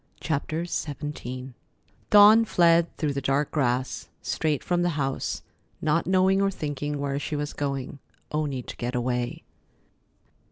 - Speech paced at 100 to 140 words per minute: Yes, slow, 135 wpm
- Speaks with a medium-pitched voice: Yes, medium, 145 Hz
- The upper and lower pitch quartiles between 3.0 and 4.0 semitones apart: Yes, average, 3.7 semitones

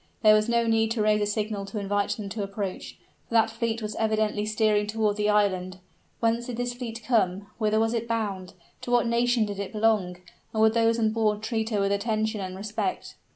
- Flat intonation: Yes, narrow, 1.7 semitones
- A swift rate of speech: Yes, fast, 215 wpm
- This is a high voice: Yes, high, 215 Hz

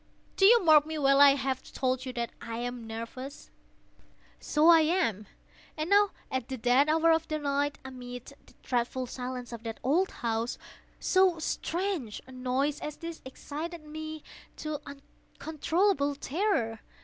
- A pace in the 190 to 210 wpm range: No, average, 155 wpm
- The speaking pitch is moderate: No, very high, 280 Hz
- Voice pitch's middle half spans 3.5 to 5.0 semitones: Yes, average, 4.2 semitones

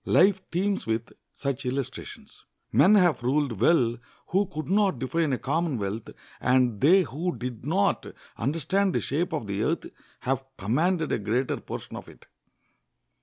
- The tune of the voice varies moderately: No, wide, 6.3 semitones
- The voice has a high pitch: No, medium, 145 Hz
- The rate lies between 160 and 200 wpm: No, average, 150 wpm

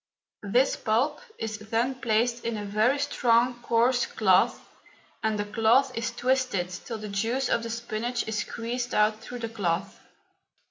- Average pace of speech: Yes, average, 155 wpm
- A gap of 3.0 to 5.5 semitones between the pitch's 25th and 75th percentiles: No, narrow, 2.4 semitones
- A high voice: Yes, high, 230 Hz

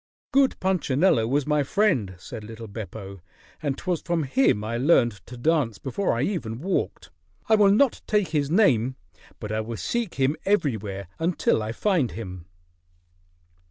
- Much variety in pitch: Yes, wide, 8.6 semitones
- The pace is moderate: Yes, average, 160 wpm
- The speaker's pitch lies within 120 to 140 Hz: Yes, low, 135 Hz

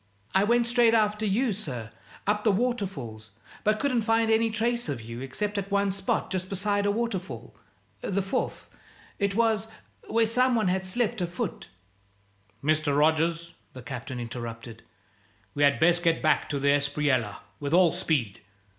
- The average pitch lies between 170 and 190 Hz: Yes, medium, 185 Hz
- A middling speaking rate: Yes, average, 165 wpm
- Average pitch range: No, wide, 7.3 semitones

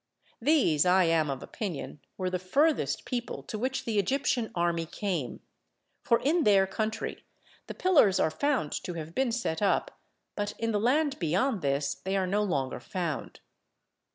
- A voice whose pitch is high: Yes, high, 195 Hz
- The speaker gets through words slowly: No, average, 165 wpm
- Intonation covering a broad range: Yes, wide, 6.4 semitones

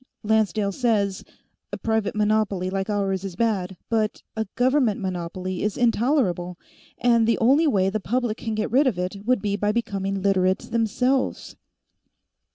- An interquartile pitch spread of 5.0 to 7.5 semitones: No, average, 3.2 semitones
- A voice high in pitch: Yes, high, 210 Hz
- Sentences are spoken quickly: No, average, 155 wpm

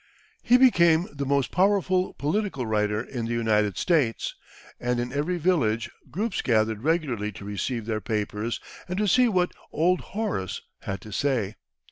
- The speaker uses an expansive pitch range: Yes, wide, 8.7 semitones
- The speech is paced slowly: No, average, 155 wpm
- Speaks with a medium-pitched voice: No, low, 130 Hz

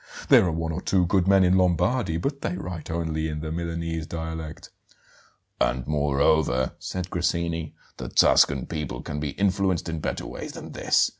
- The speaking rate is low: No, average, 175 wpm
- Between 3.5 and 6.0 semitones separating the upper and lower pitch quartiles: No, narrow, 2.5 semitones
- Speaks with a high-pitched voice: No, very low, 80 Hz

